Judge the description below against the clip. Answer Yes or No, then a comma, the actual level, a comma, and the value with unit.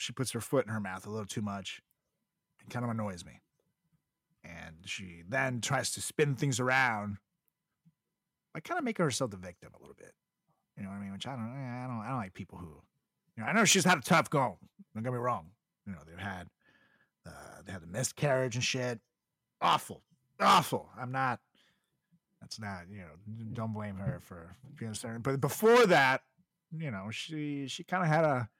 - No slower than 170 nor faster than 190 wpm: No, fast, 205 wpm